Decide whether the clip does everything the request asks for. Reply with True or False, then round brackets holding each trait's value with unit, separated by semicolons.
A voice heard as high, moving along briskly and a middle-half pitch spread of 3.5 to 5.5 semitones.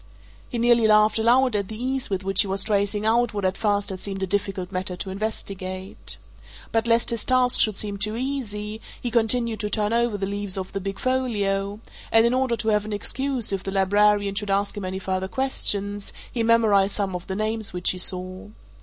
False (205 Hz; 215 wpm; 2.8 semitones)